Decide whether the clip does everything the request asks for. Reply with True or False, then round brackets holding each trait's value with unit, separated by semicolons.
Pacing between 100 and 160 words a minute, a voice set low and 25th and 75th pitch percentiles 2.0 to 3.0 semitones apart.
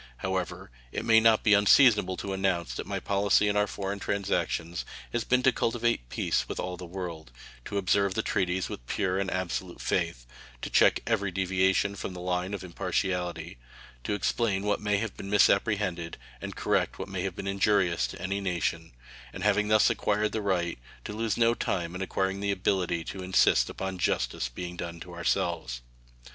False (185 wpm; 95 Hz; 2.4 semitones)